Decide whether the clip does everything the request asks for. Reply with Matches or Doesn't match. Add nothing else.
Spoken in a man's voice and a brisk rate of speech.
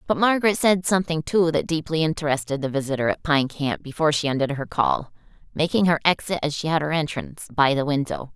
Doesn't match